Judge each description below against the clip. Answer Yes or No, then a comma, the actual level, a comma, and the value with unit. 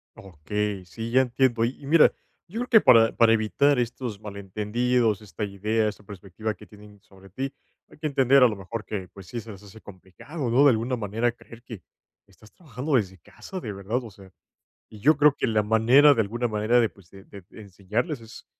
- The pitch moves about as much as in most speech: Yes, average, 3.5 semitones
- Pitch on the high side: No, low, 110 Hz